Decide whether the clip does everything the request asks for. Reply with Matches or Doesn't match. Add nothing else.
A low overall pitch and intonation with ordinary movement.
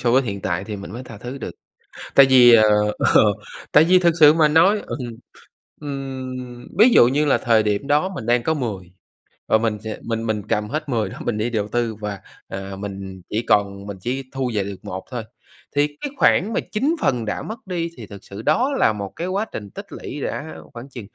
Doesn't match